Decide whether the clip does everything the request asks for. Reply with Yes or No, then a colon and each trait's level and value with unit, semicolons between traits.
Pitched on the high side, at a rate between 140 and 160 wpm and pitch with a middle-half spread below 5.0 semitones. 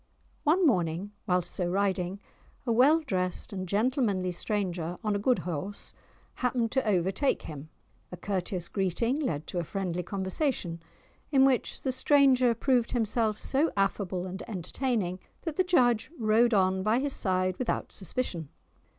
No: high, 205 Hz; average, 150 wpm; wide, 5.6 semitones